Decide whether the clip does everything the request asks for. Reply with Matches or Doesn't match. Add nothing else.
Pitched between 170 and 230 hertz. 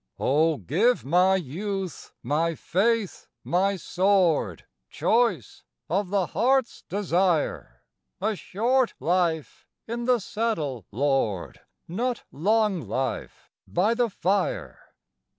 Matches